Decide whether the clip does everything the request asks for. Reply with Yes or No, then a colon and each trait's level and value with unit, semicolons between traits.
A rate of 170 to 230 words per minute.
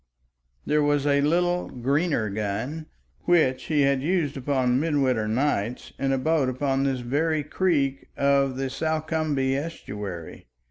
No: slow, 135 wpm